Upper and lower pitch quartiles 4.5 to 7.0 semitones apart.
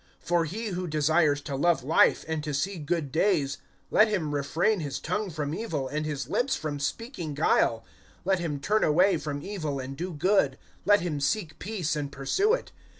Yes: average, 4.8 semitones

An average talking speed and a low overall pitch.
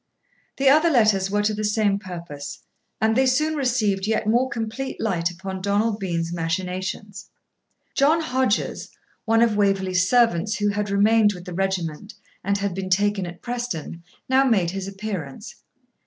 No: average, 155 wpm; high, 205 Hz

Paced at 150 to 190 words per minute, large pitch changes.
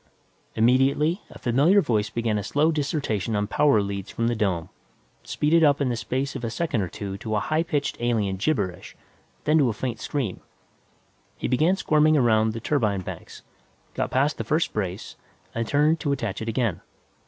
Yes: average, 185 wpm; wide, 5.7 semitones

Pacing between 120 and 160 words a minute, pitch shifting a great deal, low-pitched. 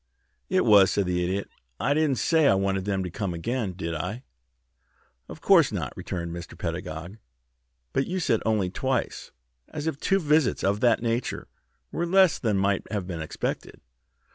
No: average, 170 wpm; wide, 6.7 semitones; low, 100 Hz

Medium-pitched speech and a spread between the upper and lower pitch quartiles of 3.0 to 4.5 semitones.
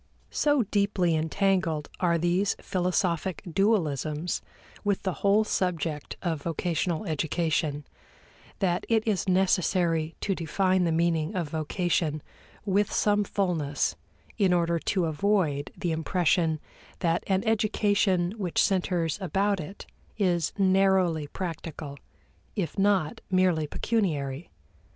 Yes: medium, 180 Hz; average, 3.4 semitones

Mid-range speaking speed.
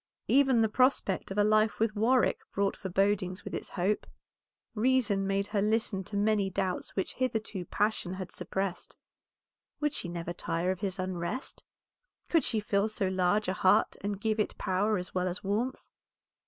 Yes: average, 170 wpm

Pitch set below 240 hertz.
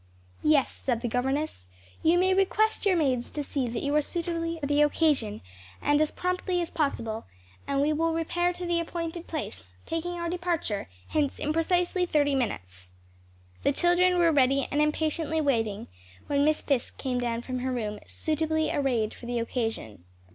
No: very high, 295 Hz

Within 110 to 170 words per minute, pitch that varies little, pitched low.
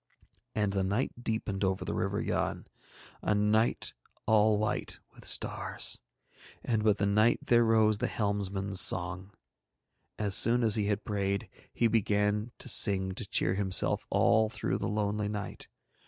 Yes: average, 155 wpm; narrow, 1.8 semitones; low, 105 Hz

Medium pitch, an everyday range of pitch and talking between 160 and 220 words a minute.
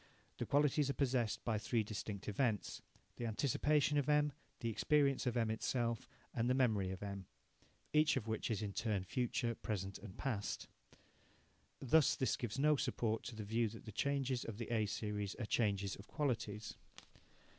No: low, 115 Hz; average, 4.2 semitones; average, 170 wpm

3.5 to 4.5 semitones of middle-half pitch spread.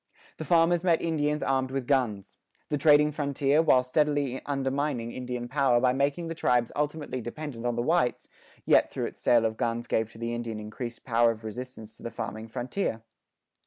Yes: average, 3.8 semitones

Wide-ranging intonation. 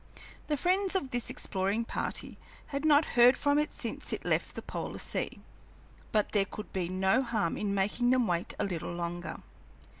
Yes: wide, 6.4 semitones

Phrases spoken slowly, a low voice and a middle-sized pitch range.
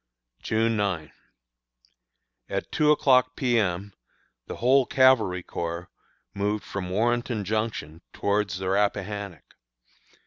Yes: slow, 105 wpm; low, 105 Hz; average, 4.2 semitones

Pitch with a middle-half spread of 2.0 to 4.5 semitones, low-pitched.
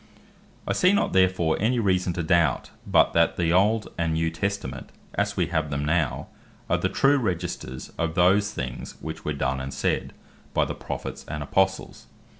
Yes: average, 3.8 semitones; very low, 85 Hz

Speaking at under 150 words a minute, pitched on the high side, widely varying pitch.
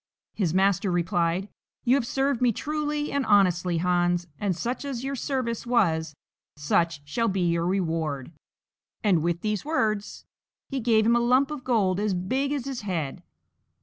No: average, 165 wpm; high, 205 Hz; wide, 6.3 semitones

